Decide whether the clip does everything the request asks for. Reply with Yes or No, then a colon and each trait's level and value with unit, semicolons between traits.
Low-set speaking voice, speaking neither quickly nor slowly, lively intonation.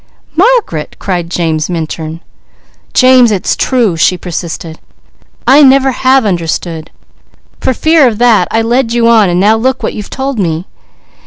No: high, 215 Hz; average, 150 wpm; wide, 7.2 semitones